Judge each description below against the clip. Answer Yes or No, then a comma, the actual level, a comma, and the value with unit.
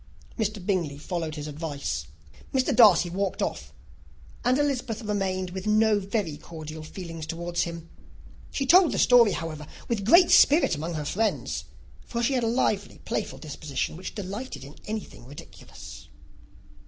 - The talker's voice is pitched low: No, high, 190 Hz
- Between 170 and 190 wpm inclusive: No, average, 150 wpm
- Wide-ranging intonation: Yes, wide, 5.9 semitones